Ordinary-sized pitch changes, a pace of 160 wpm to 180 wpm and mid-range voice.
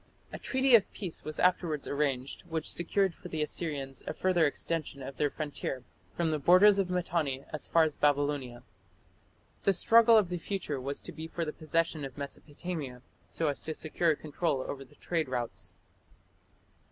Yes: average, 3.7 semitones; average, 175 wpm; medium, 155 Hz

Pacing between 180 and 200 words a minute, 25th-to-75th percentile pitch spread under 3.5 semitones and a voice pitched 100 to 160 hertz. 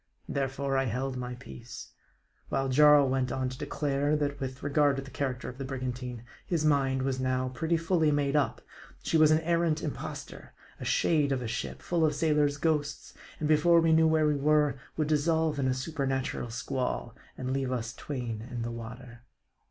Yes: average, 190 wpm; average, 2.9 semitones; medium, 140 Hz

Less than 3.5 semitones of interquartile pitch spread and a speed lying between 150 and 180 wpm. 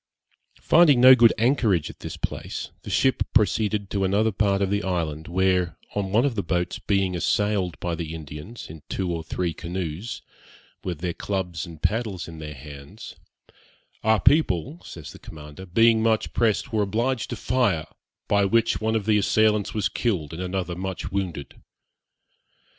No: average, 4.5 semitones; average, 170 wpm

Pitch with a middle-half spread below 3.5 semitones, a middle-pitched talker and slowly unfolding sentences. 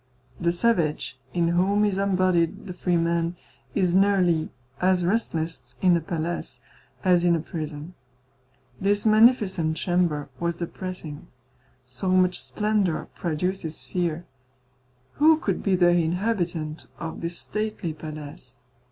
Yes: average, 2.7 semitones; medium, 175 Hz; slow, 125 wpm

